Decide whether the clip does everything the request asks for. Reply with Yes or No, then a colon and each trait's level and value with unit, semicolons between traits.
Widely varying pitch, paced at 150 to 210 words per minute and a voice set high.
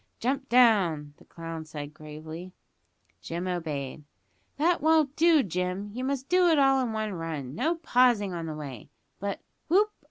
Yes: wide, 9.0 semitones; average, 160 wpm; high, 200 Hz